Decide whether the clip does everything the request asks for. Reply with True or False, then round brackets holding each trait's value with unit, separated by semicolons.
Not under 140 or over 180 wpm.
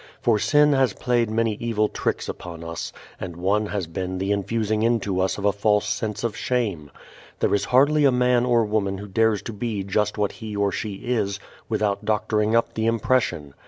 False (195 wpm)